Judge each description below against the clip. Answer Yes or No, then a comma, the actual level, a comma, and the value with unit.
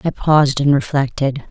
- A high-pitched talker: No, medium, 140 Hz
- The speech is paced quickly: No, average, 160 wpm